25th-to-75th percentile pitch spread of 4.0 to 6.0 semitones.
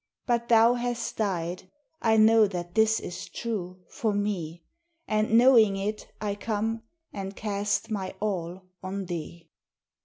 No: average, 3.3 semitones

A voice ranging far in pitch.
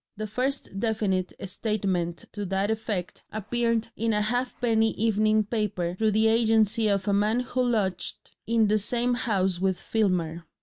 No: average, 2.8 semitones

